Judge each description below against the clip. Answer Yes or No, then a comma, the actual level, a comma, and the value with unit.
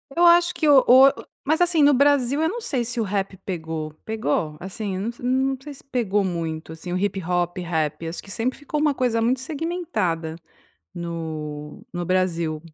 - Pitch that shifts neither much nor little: No, wide, 8.4 semitones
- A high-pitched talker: Yes, high, 205 Hz